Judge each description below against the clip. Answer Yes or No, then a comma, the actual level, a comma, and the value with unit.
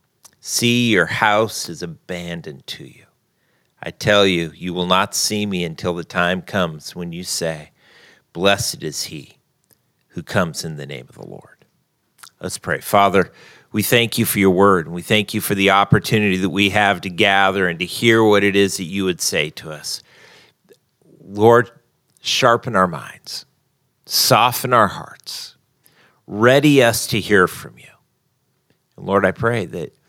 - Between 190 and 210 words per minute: No, average, 170 wpm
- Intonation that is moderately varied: Yes, average, 3.4 semitones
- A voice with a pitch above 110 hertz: No, low, 100 Hz